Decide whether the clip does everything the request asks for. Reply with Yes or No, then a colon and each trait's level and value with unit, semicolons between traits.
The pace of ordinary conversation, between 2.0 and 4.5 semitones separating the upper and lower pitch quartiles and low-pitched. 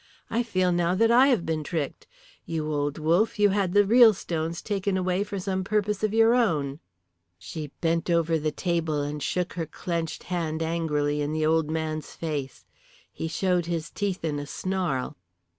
No: average, 180 wpm; average, 3.7 semitones; medium, 170 Hz